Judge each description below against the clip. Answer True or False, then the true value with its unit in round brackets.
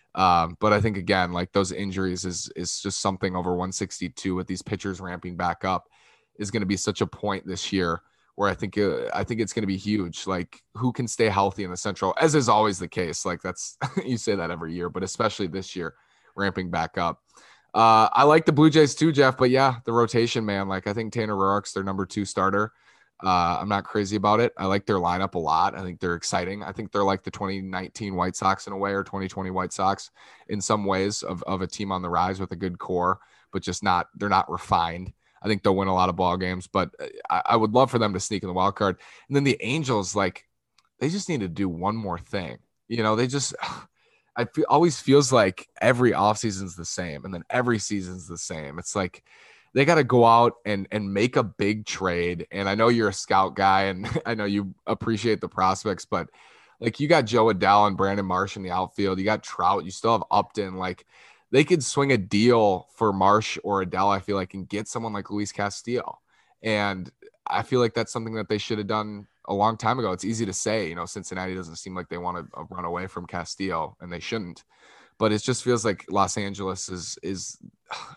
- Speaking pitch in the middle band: False (100 Hz)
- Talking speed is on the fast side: True (235 wpm)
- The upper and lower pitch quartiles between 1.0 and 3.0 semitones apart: False (3.4 semitones)